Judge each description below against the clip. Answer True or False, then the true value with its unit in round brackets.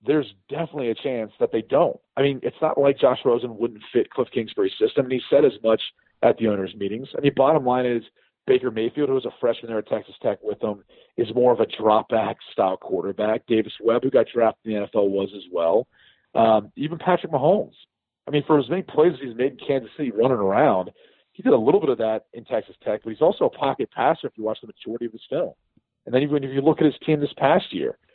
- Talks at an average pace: False (255 wpm)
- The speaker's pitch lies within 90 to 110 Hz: False (130 Hz)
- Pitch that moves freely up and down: True (6.0 semitones)